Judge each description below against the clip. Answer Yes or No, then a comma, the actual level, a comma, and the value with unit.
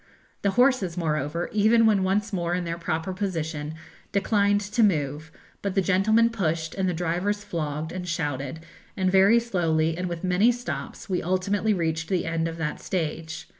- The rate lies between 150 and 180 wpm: Yes, average, 170 wpm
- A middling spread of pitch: Yes, average, 3.8 semitones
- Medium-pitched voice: Yes, medium, 180 Hz